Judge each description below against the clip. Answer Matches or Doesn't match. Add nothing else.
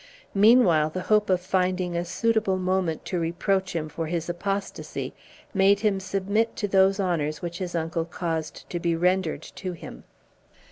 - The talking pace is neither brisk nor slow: Matches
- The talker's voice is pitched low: Doesn't match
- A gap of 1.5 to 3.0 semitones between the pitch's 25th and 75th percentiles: Matches